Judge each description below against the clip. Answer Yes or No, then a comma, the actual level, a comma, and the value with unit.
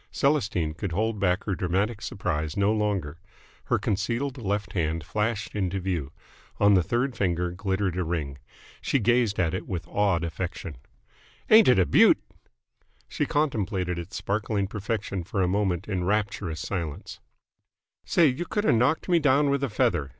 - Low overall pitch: Yes, low, 100 Hz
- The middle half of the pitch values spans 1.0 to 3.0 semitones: No, average, 4.1 semitones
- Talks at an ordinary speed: Yes, average, 165 wpm